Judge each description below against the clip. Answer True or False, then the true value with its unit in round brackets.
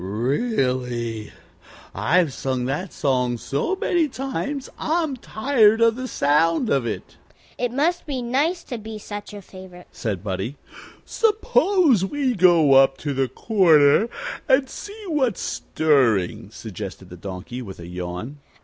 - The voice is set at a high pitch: False (180 Hz)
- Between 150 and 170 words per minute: False (140 wpm)